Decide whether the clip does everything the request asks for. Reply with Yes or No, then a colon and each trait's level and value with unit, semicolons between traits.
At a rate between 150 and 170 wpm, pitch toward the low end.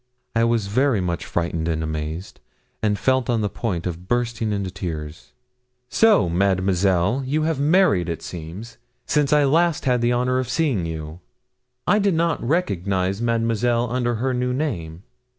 Yes: average, 160 wpm; low, 115 Hz